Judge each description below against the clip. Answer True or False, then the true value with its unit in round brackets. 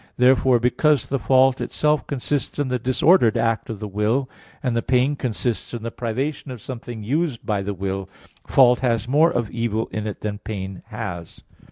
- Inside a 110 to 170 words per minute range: False (185 wpm)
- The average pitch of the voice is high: False (120 Hz)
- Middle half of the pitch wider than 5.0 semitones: False (3.5 semitones)